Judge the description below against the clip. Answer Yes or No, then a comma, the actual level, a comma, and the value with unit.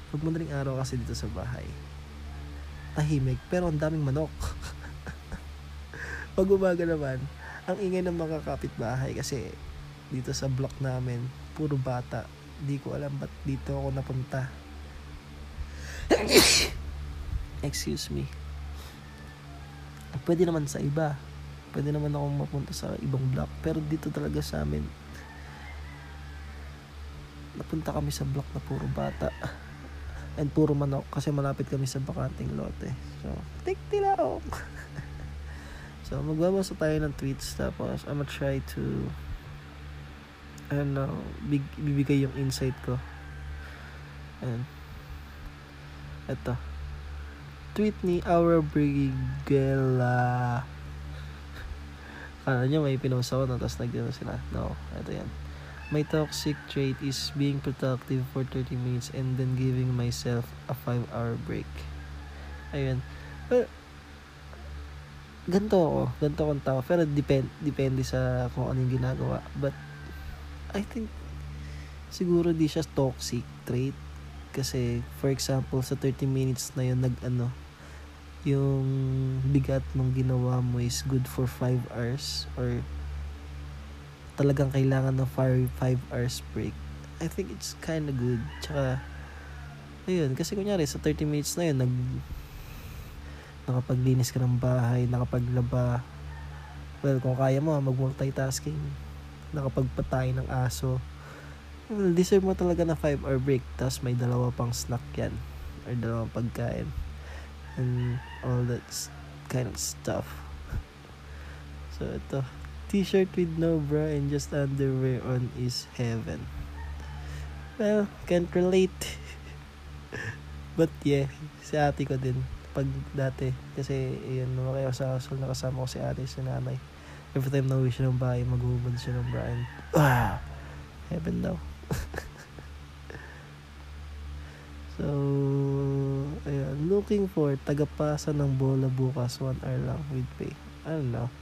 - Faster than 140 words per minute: No, average, 125 wpm